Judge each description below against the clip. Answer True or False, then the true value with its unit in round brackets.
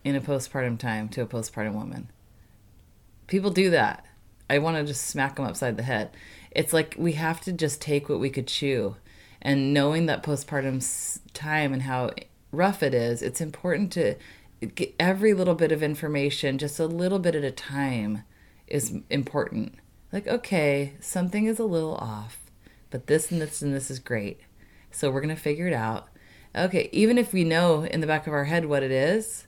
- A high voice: False (140 Hz)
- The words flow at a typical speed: True (195 wpm)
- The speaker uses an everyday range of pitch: False (6.2 semitones)